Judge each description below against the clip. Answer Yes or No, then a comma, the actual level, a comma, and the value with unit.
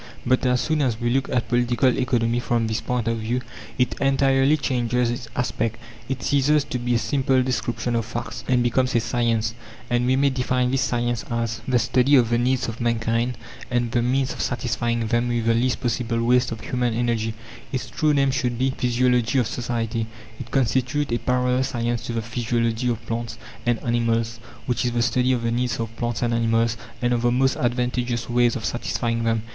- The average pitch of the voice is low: Yes, low, 120 Hz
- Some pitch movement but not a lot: No, narrow, 1.4 semitones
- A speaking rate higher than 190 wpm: Yes, fast, 205 wpm